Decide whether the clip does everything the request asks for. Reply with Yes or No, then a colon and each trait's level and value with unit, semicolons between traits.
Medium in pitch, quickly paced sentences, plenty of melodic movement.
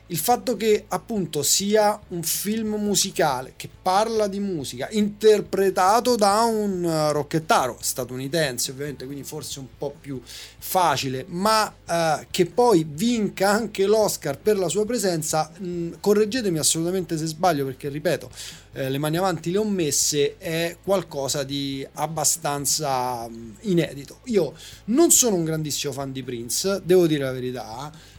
No: medium, 165 Hz; average, 145 wpm; wide, 6.1 semitones